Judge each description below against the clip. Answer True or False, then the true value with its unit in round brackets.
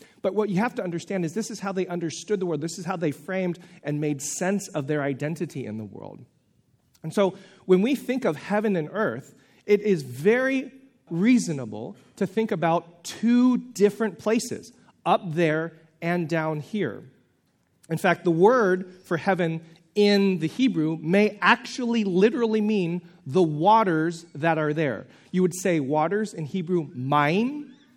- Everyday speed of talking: True (165 wpm)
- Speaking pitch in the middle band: True (180 Hz)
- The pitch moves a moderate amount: True (4.7 semitones)